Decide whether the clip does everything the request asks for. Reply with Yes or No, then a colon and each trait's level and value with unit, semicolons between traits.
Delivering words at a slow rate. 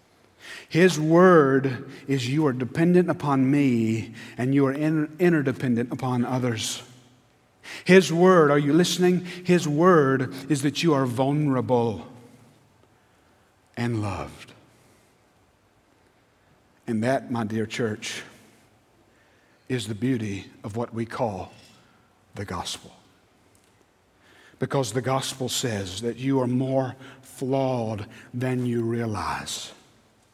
Yes: slow, 105 wpm